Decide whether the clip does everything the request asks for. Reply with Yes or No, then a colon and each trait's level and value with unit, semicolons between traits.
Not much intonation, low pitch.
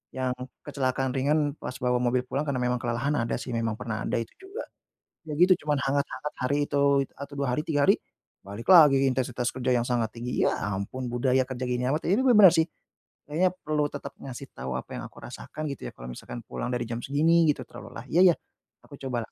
No: average, 3.1 semitones; low, 130 Hz